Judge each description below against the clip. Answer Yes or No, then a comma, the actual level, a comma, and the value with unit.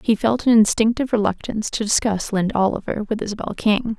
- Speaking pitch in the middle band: No, high, 215 Hz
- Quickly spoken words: No, average, 180 wpm